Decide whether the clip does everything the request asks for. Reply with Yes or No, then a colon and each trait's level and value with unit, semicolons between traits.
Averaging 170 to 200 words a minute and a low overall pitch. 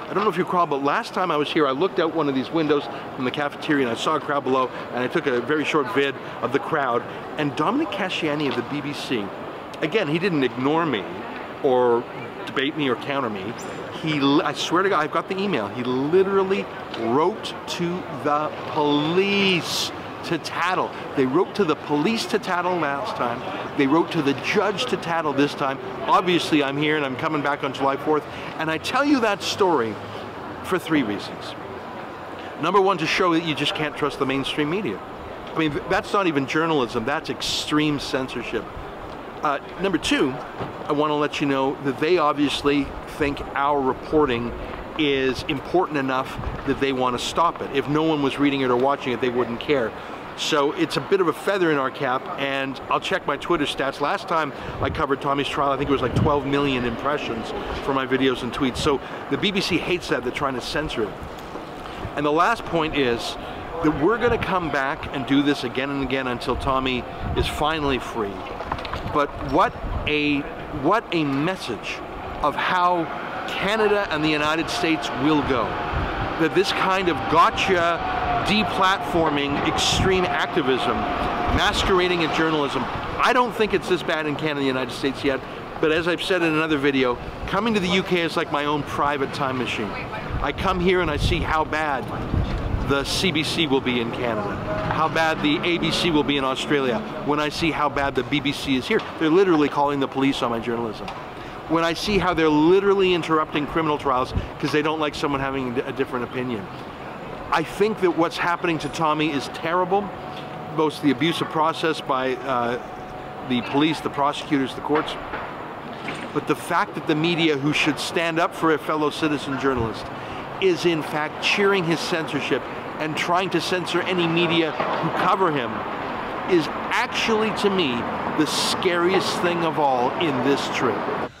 No: average, 185 wpm; medium, 150 Hz